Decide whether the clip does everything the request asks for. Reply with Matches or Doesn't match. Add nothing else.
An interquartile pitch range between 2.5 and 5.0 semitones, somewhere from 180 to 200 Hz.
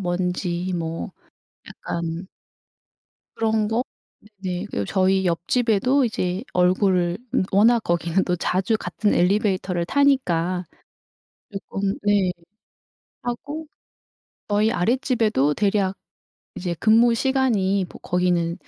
Matches